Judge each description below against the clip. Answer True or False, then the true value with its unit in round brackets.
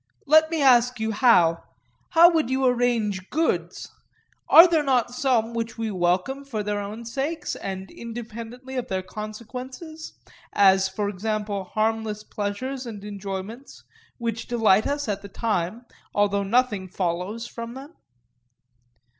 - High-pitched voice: True (225 Hz)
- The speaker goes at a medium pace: False (130 wpm)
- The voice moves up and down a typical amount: True (4.0 semitones)